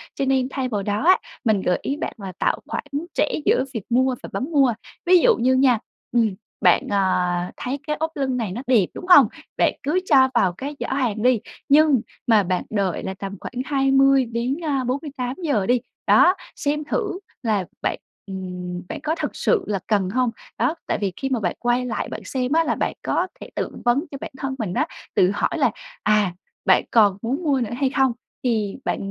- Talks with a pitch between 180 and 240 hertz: No, very high, 250 Hz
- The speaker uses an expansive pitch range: No, average, 4.9 semitones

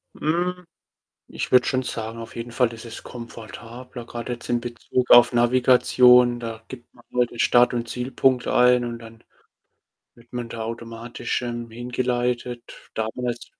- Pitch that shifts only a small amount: Yes, narrow, 1.1 semitones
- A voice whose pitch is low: Yes, low, 120 Hz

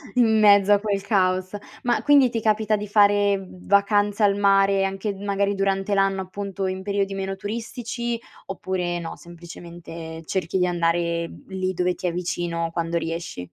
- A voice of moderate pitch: No, high, 195 Hz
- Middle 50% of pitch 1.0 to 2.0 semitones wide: No, narrow, 2.6 semitones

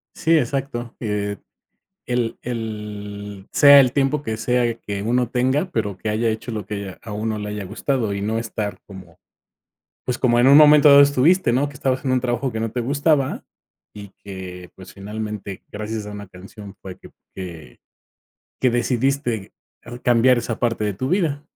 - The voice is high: No, low, 115 Hz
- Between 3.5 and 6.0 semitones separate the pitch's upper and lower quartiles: Yes, average, 4.1 semitones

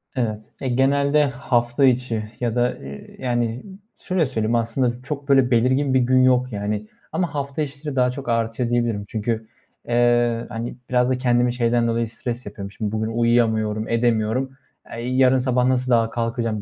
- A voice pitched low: Yes, low, 120 Hz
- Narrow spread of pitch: Yes, narrow, 2.1 semitones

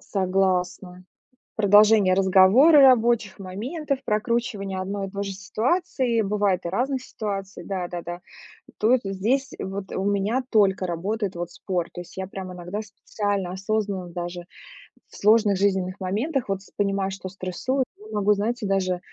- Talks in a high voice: Yes, high, 195 Hz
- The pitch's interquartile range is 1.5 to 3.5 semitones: Yes, narrow, 2.6 semitones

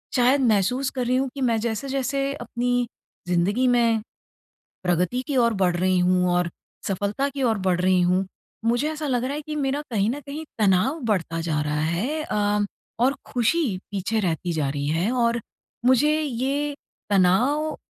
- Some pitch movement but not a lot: No, wide, 6.6 semitones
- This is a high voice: Yes, high, 235 Hz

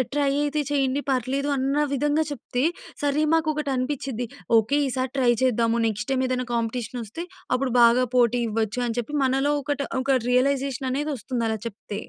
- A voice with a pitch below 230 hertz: No, very high, 260 Hz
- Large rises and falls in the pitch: No, average, 2.9 semitones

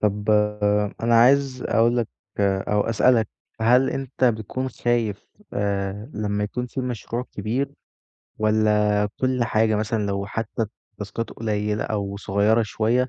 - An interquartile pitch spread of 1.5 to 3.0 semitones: Yes, narrow, 2.6 semitones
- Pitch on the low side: Yes, low, 110 Hz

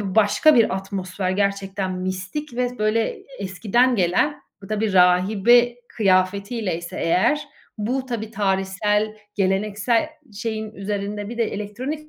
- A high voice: Yes, high, 205 Hz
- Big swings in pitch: No, average, 3.4 semitones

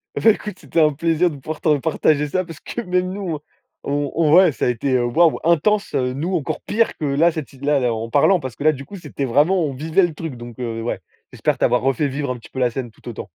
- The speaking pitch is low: No, medium, 150 Hz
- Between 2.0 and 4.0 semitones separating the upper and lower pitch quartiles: No, average, 4.7 semitones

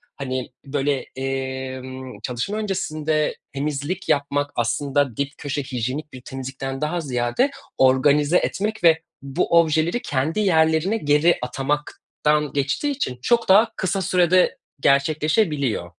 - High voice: No, medium, 145 Hz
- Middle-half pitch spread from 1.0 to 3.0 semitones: No, average, 4.1 semitones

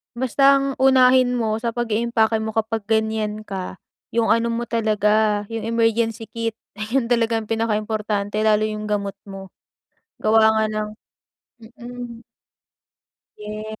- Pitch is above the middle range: Yes, high, 220 Hz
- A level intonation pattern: Yes, narrow, 1.5 semitones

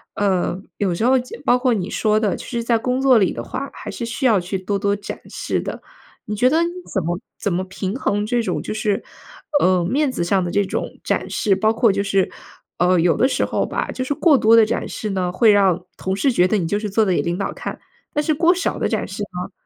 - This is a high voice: Yes, high, 205 Hz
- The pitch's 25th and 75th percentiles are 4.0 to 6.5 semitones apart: Yes, average, 4.5 semitones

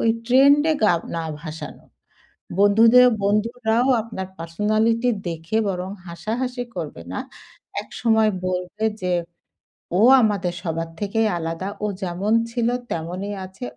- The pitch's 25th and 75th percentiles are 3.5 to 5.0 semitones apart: Yes, average, 4.2 semitones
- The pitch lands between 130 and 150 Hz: No, high, 205 Hz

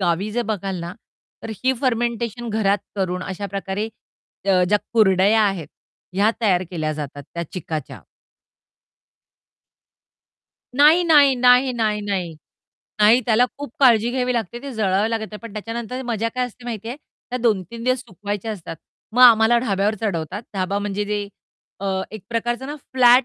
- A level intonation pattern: No, average, 3.8 semitones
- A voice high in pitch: Yes, high, 215 Hz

